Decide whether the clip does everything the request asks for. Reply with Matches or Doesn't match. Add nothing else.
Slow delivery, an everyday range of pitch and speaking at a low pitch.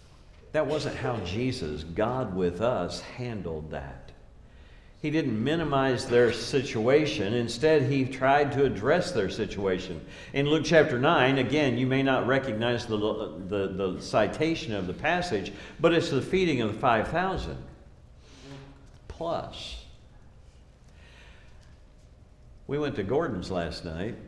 Doesn't match